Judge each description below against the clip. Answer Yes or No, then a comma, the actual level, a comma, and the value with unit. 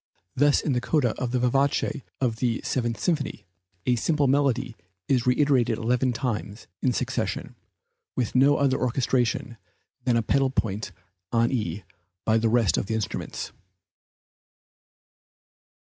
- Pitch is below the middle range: Yes, low, 125 Hz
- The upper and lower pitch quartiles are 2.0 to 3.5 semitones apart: Yes, average, 2.8 semitones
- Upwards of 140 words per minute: No, slow, 135 wpm